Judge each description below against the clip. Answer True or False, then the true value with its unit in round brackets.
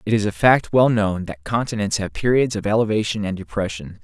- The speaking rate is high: True (210 wpm)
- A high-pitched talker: False (105 Hz)